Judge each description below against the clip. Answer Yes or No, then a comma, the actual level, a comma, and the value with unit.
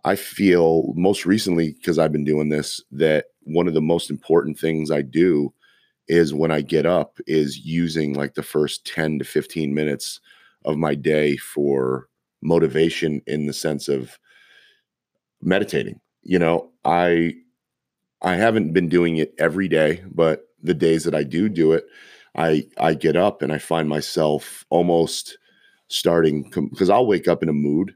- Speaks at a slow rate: No, average, 165 wpm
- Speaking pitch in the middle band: No, very low, 80 Hz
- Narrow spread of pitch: Yes, narrow, 2.1 semitones